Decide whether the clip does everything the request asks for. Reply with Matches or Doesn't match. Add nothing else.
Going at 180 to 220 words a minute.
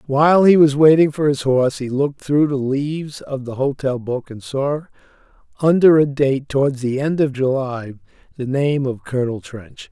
Matches